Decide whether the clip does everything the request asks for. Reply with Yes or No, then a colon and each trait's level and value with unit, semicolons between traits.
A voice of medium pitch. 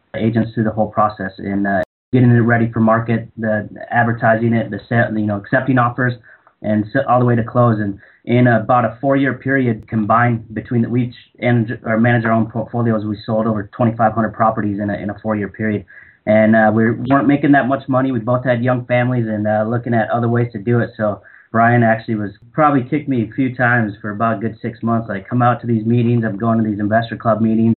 No: low, 115 Hz